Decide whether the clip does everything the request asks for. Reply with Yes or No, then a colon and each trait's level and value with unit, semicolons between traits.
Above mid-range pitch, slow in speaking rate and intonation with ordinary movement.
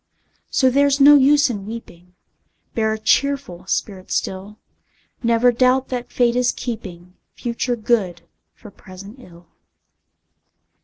Yes: high, 230 Hz; slow, 120 wpm; average, 5.0 semitones